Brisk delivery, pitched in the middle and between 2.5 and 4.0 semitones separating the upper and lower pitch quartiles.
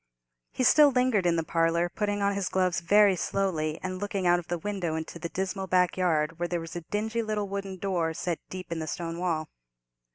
Yes: fast, 215 wpm; medium, 180 Hz; average, 3.0 semitones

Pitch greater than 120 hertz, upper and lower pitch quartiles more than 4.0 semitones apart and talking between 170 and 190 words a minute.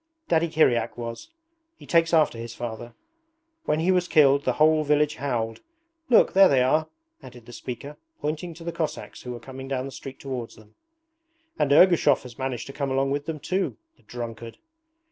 Yes: medium, 140 Hz; average, 4.4 semitones; average, 185 wpm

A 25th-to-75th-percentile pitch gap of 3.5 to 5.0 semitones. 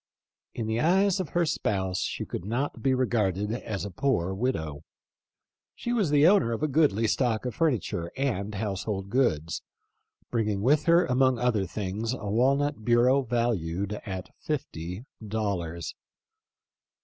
No: wide, 5.5 semitones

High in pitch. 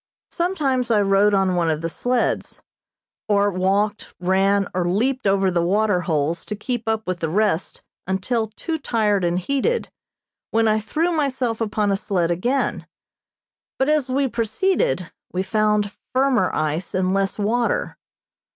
Yes: high, 205 Hz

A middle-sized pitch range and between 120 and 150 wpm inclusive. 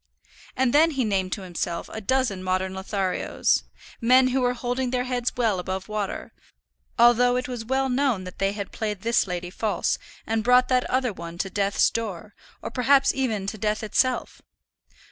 No: average, 4.5 semitones; average, 175 wpm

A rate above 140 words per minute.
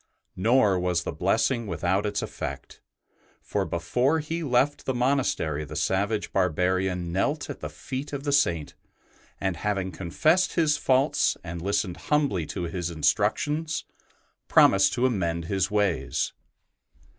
No: slow, 135 wpm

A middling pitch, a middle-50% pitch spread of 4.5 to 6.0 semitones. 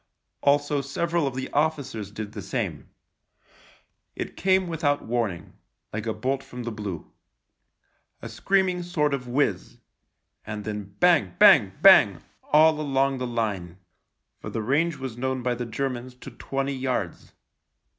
No: low, 130 Hz; average, 4.8 semitones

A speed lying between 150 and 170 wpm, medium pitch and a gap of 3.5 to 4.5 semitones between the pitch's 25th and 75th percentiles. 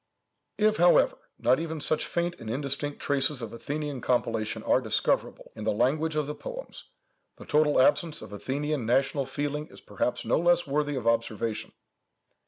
Yes: average, 165 wpm; medium, 145 Hz; average, 3.9 semitones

